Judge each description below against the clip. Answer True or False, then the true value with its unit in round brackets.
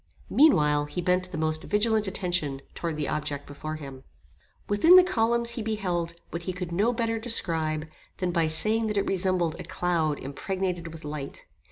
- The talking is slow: False (175 wpm)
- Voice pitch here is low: False (175 Hz)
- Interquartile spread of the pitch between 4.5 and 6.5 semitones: True (5.1 semitones)